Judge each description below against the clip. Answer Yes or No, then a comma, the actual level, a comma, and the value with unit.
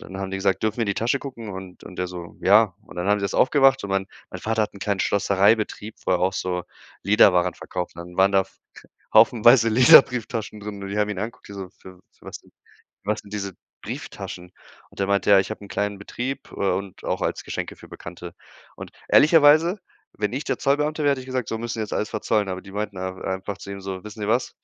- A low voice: Yes, low, 100 Hz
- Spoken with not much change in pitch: No, average, 3.1 semitones